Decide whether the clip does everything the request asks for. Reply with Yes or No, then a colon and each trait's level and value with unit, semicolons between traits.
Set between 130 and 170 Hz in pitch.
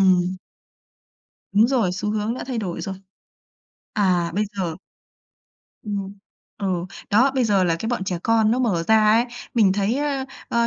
No: high, 210 Hz